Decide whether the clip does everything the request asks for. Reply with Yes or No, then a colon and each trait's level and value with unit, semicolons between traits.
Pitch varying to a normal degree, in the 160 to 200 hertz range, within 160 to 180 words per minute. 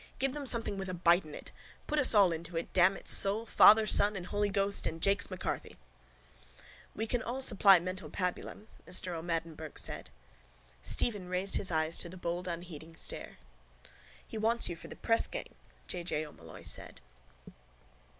Yes: average, 3.6 semitones; medium, 185 Hz; average, 175 wpm